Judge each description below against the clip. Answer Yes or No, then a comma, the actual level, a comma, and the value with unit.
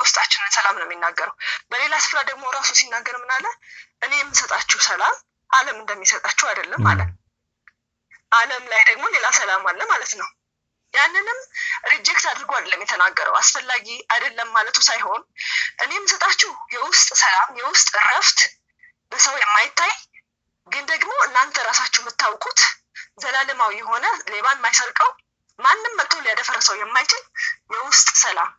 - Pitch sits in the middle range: No, very high, 270 Hz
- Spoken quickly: Yes, fast, 120 wpm